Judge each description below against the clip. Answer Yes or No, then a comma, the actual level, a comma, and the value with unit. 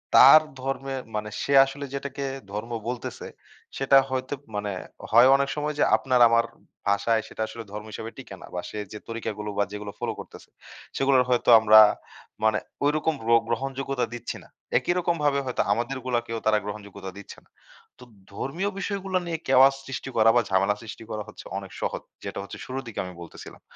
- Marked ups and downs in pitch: No, average, 4.2 semitones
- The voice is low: Yes, low, 120 Hz